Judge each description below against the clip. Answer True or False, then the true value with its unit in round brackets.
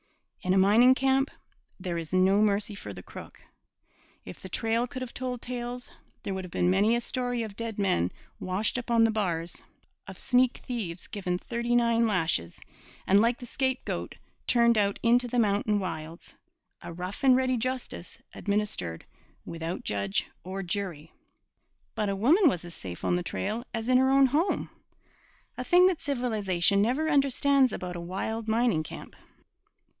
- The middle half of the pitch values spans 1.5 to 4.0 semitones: False (5.1 semitones)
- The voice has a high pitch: True (220 Hz)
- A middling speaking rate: True (170 wpm)